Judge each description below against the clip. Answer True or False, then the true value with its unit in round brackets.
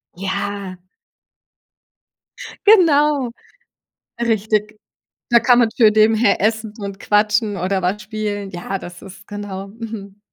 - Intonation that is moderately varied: False (2.3 semitones)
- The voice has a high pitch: True (210 Hz)